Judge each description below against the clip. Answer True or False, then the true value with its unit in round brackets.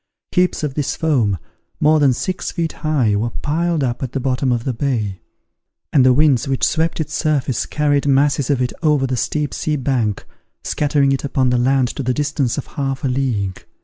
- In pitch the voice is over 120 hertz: True (135 Hz)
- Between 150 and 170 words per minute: False (200 wpm)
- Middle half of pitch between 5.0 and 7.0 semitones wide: False (2.9 semitones)